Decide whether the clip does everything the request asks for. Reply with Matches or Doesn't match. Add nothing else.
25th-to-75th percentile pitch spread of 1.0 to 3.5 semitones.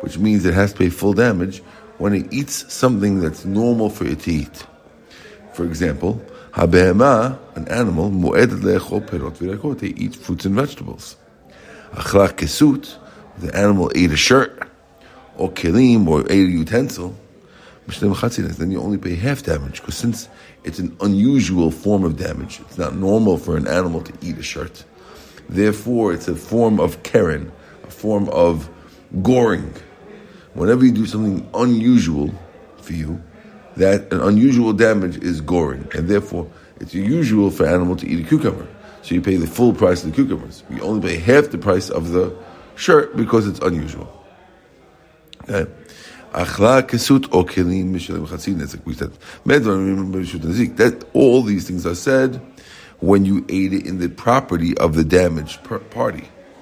Doesn't match